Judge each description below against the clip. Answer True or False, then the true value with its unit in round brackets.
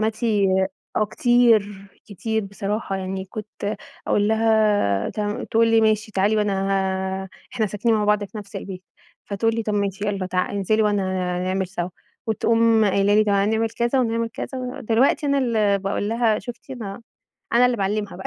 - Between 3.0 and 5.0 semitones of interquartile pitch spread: False (2.4 semitones)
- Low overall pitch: False (210 Hz)